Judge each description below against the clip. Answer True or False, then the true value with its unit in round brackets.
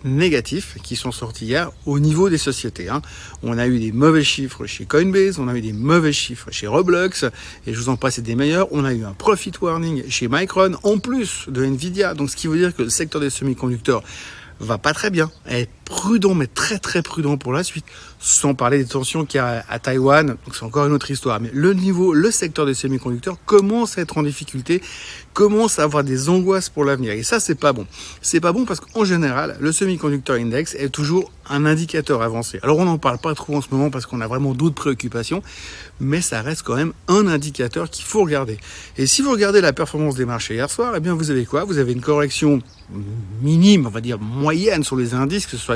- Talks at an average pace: False (235 wpm)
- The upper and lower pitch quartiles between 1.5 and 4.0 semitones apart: False (5.2 semitones)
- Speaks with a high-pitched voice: False (145 Hz)